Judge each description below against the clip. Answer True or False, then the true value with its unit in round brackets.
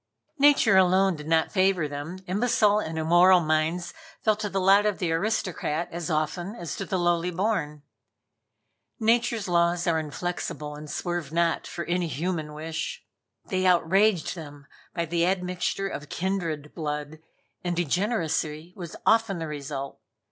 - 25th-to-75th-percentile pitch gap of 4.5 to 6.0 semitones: False (3.4 semitones)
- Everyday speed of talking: True (150 wpm)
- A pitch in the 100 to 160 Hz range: False (175 Hz)